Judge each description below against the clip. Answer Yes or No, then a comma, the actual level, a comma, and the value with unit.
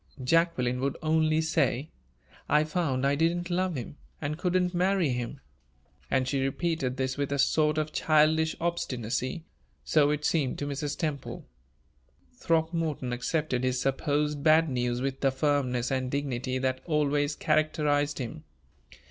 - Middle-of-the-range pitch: Yes, medium, 145 Hz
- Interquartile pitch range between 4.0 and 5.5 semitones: No, average, 3.3 semitones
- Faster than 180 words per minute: No, average, 140 wpm